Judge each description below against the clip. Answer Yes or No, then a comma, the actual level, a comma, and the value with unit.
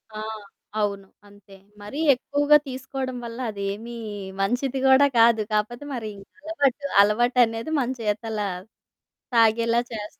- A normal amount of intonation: Yes, average, 3.7 semitones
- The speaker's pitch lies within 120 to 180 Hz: No, high, 230 Hz